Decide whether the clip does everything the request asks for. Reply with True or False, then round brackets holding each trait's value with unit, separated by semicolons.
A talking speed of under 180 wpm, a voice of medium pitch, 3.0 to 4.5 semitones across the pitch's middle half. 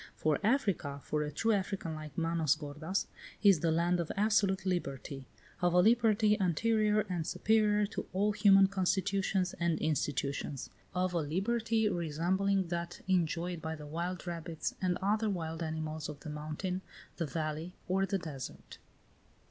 True (150 wpm; 175 Hz; 4.0 semitones)